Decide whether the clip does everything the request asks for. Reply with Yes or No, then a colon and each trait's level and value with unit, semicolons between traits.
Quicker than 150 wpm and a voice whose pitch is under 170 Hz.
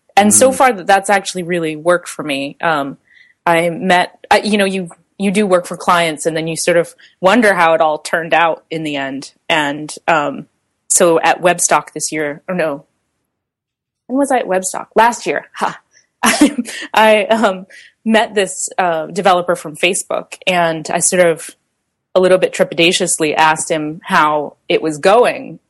No: average, 175 wpm; medium, 180 Hz